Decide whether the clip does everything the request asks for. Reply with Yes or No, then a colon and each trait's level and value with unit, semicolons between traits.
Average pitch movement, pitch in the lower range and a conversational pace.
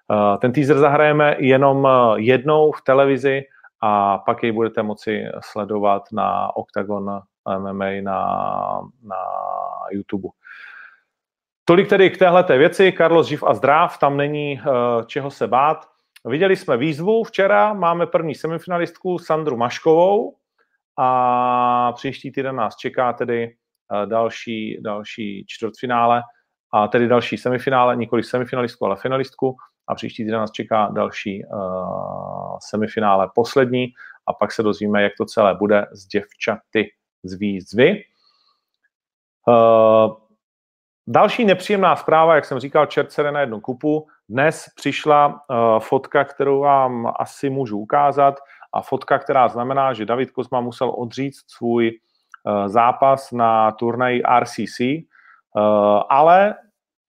Yes: average, 4.8 semitones; low, 125 Hz; average, 125 wpm